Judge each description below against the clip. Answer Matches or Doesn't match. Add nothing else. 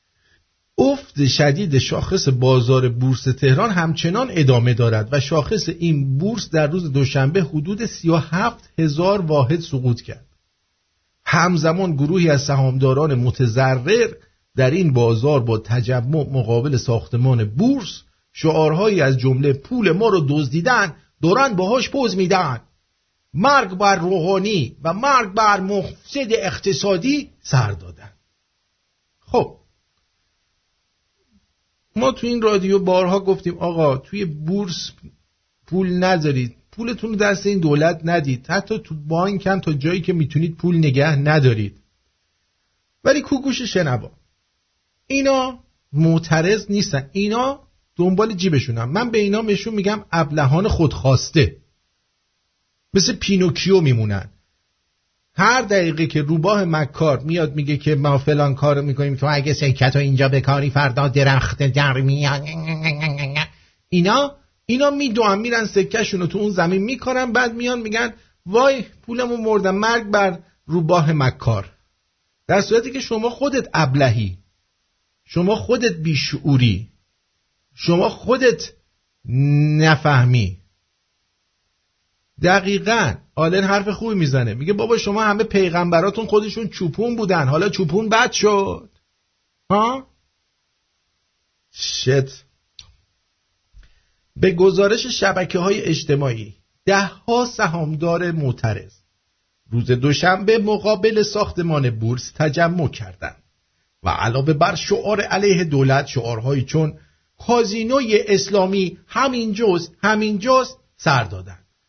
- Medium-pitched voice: Matches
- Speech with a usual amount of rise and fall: Doesn't match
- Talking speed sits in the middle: Doesn't match